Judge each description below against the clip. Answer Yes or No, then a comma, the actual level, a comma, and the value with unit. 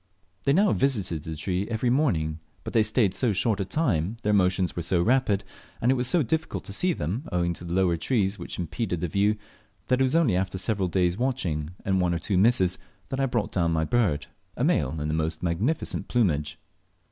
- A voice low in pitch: Yes, very low, 95 Hz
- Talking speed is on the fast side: Yes, fast, 215 wpm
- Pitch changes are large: Yes, wide, 6.0 semitones